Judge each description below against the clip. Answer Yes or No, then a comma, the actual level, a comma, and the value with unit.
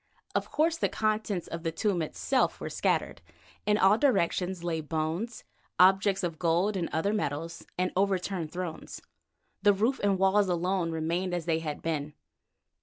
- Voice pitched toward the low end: No, medium, 180 Hz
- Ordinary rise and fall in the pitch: Yes, average, 3.5 semitones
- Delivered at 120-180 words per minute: Yes, average, 160 wpm